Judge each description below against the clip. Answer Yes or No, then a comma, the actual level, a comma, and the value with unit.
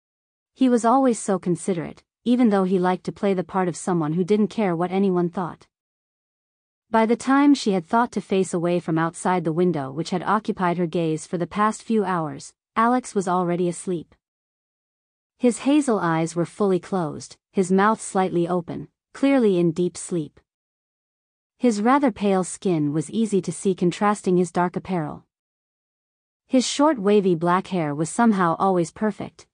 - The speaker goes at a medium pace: Yes, average, 170 wpm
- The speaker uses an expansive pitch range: No, average, 3.4 semitones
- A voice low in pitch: No, medium, 185 Hz